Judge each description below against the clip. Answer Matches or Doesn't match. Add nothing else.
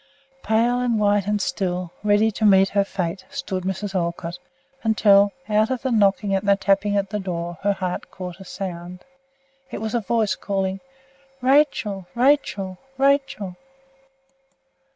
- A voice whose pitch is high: Matches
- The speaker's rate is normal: Matches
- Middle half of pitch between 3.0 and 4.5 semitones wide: Doesn't match